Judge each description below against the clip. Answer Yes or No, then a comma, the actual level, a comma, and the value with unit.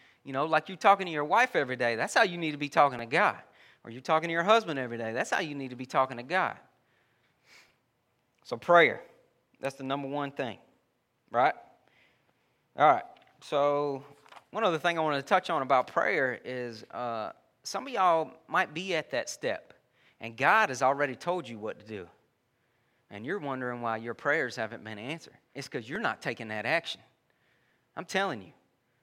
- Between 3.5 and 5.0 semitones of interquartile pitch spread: Yes, average, 4.7 semitones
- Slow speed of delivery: No, average, 195 wpm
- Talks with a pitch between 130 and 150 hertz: Yes, low, 135 Hz